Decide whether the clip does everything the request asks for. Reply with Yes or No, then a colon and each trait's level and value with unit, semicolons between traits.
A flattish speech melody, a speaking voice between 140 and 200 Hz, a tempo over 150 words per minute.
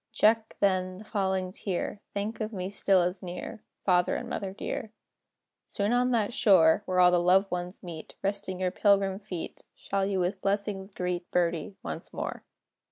Yes: narrow, 2.1 semitones; high, 190 Hz; average, 170 wpm